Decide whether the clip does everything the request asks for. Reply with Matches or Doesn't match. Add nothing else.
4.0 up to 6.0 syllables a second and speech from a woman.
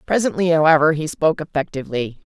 Doesn't match